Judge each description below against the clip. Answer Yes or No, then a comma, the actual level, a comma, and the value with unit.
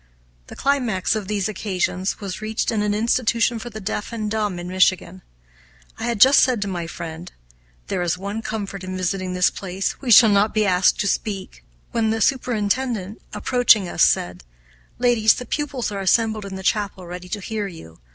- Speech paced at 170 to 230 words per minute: Yes, average, 190 wpm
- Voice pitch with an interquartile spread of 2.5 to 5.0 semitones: Yes, average, 3.1 semitones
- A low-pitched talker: No, high, 205 Hz